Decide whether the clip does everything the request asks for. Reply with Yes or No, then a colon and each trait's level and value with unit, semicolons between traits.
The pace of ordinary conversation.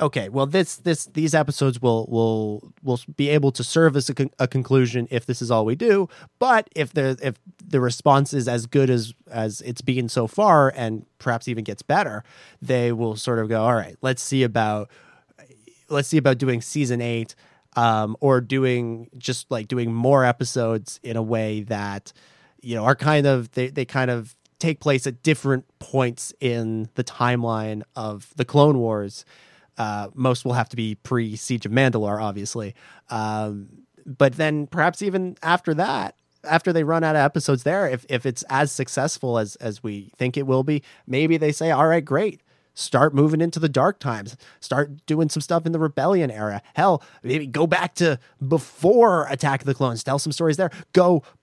Yes: average, 190 wpm